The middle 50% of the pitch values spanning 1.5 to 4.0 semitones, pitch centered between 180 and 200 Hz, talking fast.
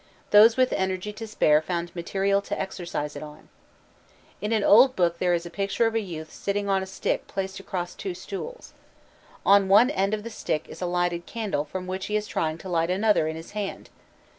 Yes: average, 3.3 semitones; high, 190 Hz; fast, 215 wpm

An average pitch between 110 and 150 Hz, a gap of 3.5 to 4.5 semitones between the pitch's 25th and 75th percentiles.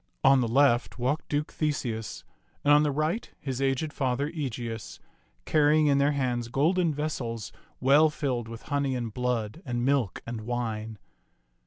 Yes: low, 135 Hz; average, 3.8 semitones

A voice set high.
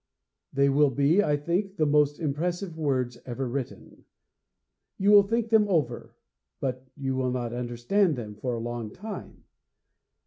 No: medium, 140 Hz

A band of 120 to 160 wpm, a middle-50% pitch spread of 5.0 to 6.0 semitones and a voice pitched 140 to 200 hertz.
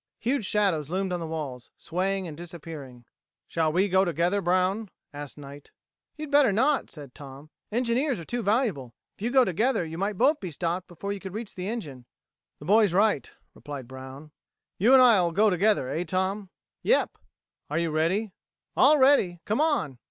No: average, 180 wpm; wide, 5.6 semitones; medium, 185 Hz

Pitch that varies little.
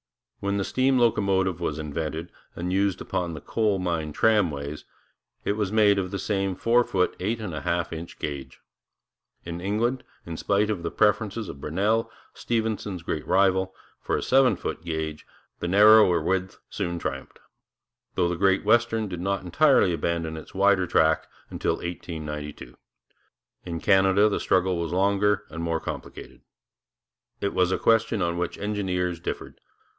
No: average, 3.5 semitones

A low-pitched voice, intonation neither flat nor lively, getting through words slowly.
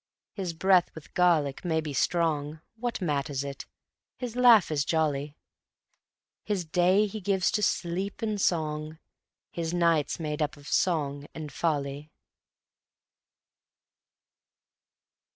No: medium, 160 Hz; average, 3.9 semitones; slow, 115 wpm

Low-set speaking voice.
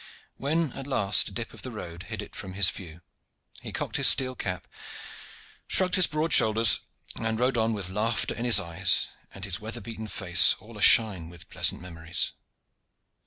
Yes: low, 105 Hz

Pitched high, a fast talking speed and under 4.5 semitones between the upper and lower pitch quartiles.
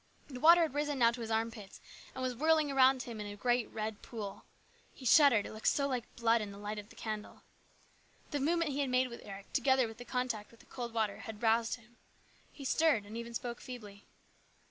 Yes: high, 235 Hz; fast, 225 wpm; average, 3.3 semitones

